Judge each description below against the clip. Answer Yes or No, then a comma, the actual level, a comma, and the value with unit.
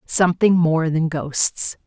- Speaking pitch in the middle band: Yes, medium, 165 Hz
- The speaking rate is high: No, slow, 130 wpm